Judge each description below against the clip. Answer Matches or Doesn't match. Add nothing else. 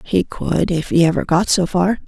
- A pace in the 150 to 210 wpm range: Matches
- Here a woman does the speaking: Matches